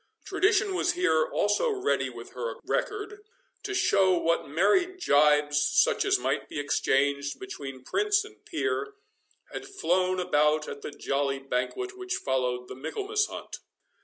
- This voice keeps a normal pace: Yes, average, 145 wpm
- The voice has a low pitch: No, medium, 185 Hz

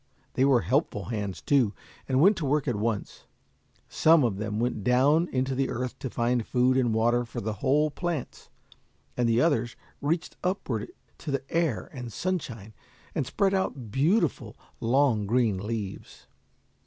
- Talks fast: No, average, 160 wpm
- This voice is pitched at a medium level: No, low, 125 Hz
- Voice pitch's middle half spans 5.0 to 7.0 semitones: No, average, 4.4 semitones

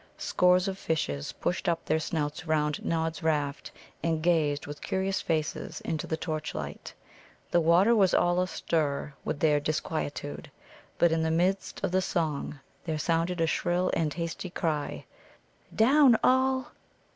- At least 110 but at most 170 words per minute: Yes, average, 145 wpm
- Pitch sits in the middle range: Yes, medium, 165 Hz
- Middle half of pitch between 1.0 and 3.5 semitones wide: Yes, average, 2.9 semitones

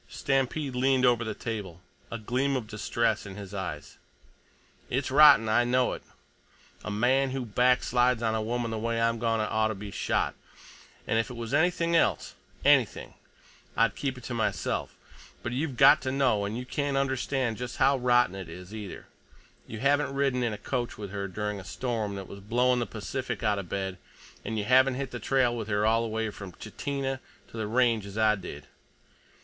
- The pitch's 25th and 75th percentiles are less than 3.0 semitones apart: No, average, 3.4 semitones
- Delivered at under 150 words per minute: No, average, 190 wpm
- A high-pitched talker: No, low, 115 Hz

